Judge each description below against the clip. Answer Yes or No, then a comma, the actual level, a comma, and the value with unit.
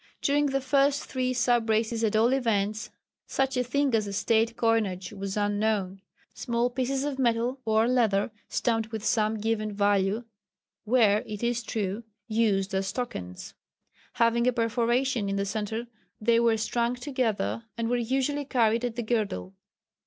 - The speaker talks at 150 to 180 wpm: Yes, average, 160 wpm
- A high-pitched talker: Yes, high, 230 Hz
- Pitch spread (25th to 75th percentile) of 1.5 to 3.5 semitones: Yes, average, 2.7 semitones